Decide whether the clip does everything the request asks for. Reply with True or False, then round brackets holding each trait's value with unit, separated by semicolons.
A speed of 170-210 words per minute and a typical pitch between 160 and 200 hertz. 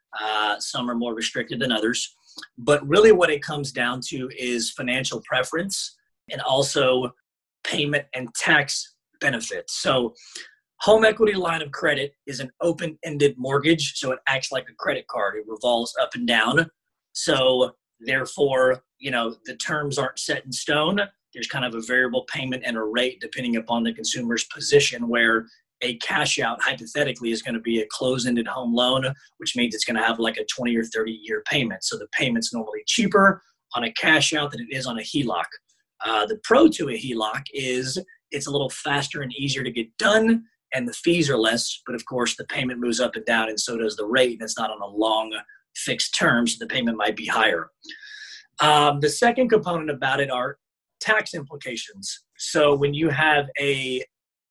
False (190 wpm; 130 Hz)